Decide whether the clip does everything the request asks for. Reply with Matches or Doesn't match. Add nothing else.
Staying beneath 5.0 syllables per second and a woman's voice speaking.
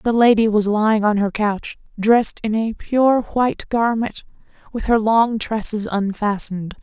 Matches